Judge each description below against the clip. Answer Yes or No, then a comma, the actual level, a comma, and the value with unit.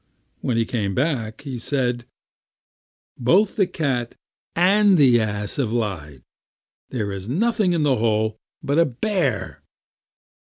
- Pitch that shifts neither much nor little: No, wide, 7.3 semitones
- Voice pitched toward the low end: Yes, low, 125 Hz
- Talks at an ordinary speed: No, slow, 130 wpm